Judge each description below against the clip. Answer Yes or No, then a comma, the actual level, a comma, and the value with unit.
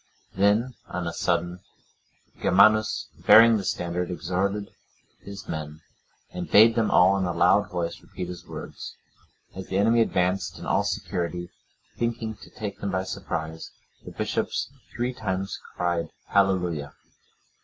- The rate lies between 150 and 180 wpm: No, average, 140 wpm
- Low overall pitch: Yes, very low, 95 Hz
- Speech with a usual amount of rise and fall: Yes, average, 3.1 semitones